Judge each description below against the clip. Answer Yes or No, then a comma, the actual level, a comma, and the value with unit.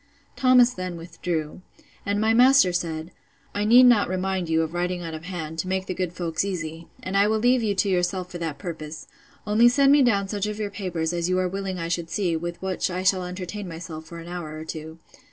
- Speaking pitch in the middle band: Yes, medium, 180 Hz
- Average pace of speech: No, fast, 230 wpm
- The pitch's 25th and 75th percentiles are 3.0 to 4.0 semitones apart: Yes, average, 3.3 semitones